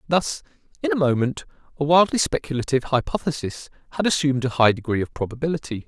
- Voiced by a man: Yes, male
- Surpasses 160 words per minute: No, average, 155 wpm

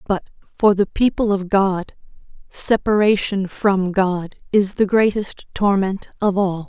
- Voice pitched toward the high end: Yes, high, 195 Hz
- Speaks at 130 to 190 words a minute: Yes, slow, 135 wpm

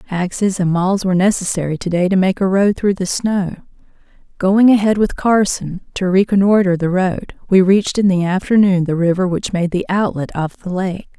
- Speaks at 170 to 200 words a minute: Yes, average, 190 wpm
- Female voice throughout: Yes, female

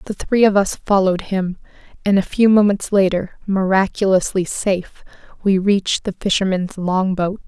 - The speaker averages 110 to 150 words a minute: Yes, average, 145 wpm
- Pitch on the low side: No, high, 195 Hz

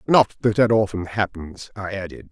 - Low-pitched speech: Yes, low, 100 Hz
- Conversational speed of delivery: Yes, average, 180 wpm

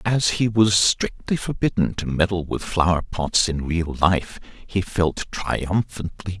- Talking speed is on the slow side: No, average, 160 wpm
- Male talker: Yes, male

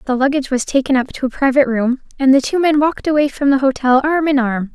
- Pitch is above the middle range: Yes, very high, 270 Hz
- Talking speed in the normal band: No, fast, 265 wpm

